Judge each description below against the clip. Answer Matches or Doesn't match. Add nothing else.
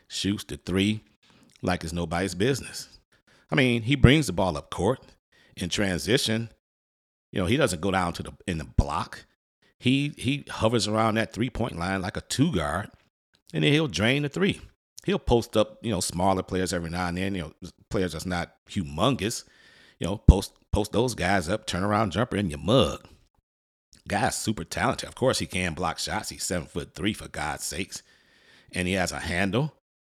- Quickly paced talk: Doesn't match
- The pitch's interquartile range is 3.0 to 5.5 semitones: Matches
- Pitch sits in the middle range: Doesn't match